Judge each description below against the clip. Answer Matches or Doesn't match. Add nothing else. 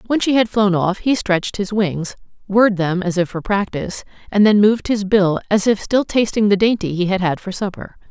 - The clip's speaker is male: Doesn't match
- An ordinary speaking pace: Doesn't match